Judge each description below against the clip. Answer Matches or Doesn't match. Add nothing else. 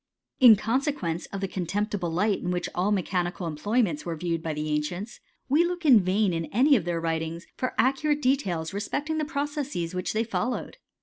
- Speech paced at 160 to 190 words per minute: Matches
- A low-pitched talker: Doesn't match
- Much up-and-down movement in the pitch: Matches